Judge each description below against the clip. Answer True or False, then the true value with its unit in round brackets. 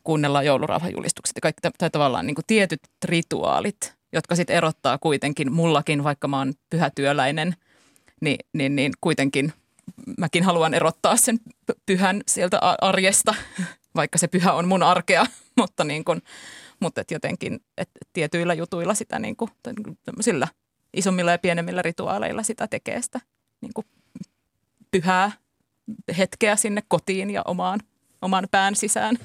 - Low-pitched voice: False (175 Hz)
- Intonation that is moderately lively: True (4.7 semitones)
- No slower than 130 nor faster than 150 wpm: True (140 wpm)